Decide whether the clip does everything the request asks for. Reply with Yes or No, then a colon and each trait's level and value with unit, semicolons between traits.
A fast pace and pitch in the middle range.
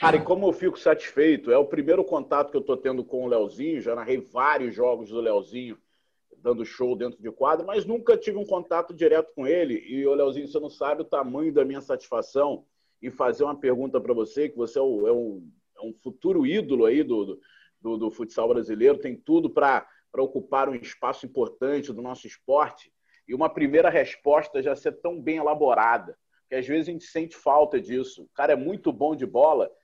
Yes: fast, 210 wpm; medium, 160 Hz